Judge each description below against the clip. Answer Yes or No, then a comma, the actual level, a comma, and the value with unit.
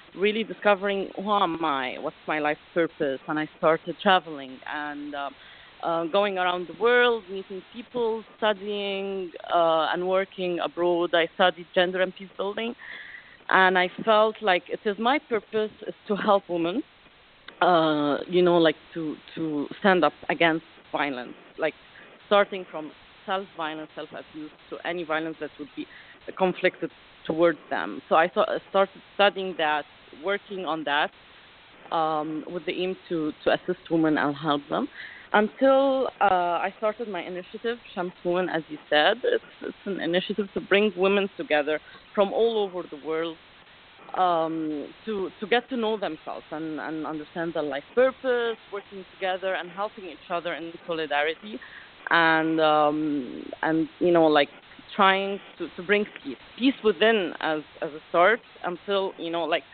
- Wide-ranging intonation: No, average, 4.1 semitones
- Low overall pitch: No, medium, 180 Hz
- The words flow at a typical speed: Yes, average, 155 wpm